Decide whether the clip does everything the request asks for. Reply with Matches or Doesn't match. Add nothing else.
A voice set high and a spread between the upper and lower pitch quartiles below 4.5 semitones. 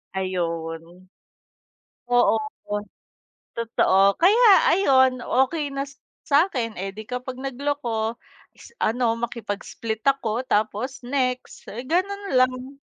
Matches